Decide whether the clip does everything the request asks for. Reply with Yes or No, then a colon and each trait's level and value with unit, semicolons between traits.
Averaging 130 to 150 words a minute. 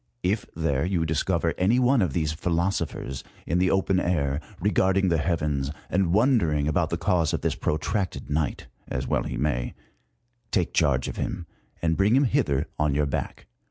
No: average, 185 wpm